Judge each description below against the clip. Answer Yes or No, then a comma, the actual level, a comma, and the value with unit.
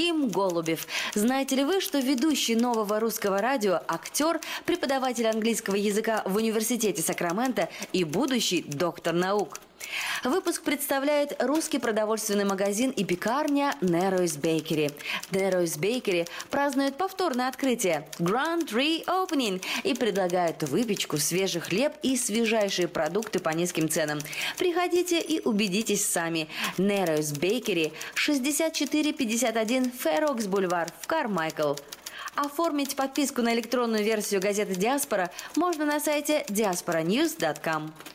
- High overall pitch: Yes, high, 220 Hz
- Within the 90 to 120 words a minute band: Yes, slow, 110 wpm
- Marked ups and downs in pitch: Yes, wide, 8.1 semitones